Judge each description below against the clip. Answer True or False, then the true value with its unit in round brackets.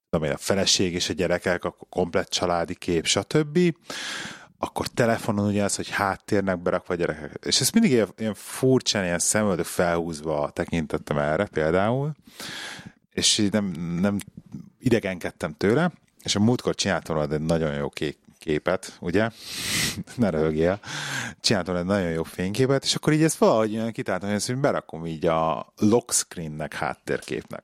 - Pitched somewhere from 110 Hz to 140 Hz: False (95 Hz)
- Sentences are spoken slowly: False (150 wpm)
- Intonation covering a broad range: True (5.8 semitones)